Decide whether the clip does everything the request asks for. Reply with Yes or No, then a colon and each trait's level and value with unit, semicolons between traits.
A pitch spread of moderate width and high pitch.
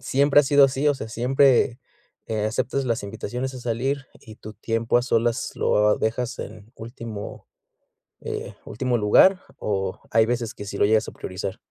No: average, 3.4 semitones; low, 115 Hz